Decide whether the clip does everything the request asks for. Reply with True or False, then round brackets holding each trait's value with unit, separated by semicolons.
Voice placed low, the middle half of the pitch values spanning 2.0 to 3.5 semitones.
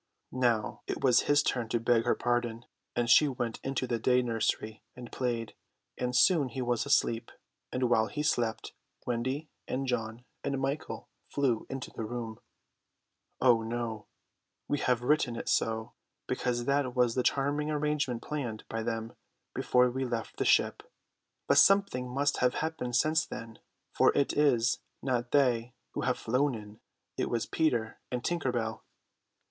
True (125 Hz; 2.8 semitones)